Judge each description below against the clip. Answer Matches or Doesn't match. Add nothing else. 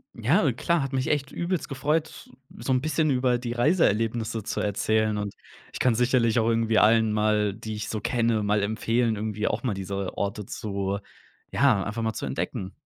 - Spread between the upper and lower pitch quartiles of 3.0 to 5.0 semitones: Matches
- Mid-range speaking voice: Doesn't match